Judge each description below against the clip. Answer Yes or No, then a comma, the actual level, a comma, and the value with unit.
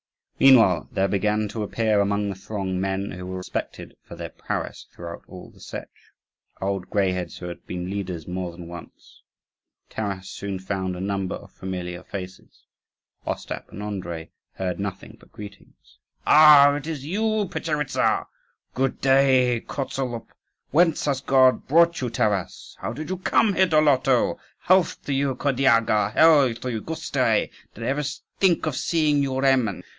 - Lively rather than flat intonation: Yes, wide, 6.7 semitones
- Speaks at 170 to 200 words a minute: No, average, 160 wpm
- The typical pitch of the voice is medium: No, low, 110 Hz